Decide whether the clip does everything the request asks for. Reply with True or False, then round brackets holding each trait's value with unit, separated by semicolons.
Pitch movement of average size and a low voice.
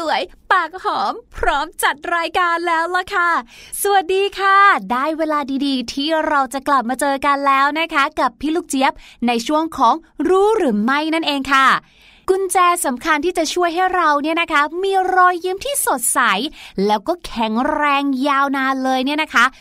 False (4.7 semitones; 310 Hz)